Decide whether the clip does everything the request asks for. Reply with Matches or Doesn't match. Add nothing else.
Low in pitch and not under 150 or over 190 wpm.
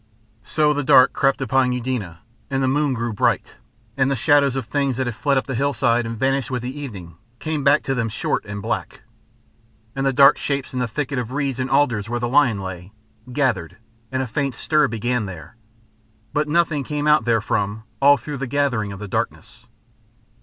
Doesn't match